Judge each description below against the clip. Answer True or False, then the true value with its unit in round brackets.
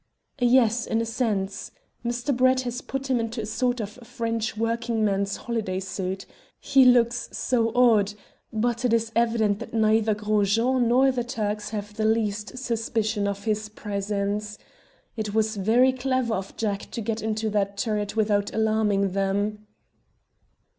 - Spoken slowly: False (155 wpm)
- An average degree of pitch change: False (2.3 semitones)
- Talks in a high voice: True (220 Hz)